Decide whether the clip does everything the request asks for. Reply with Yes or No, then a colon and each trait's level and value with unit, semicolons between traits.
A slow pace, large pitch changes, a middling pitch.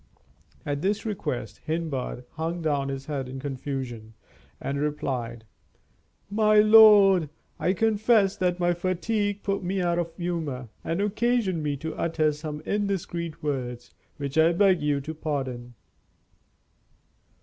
Yes: slow, 130 wpm; wide, 5.7 semitones; medium, 160 Hz